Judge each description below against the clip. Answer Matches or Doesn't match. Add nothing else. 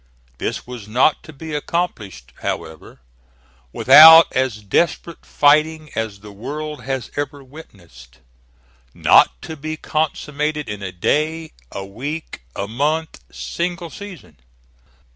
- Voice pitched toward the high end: Doesn't match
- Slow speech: Matches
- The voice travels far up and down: Matches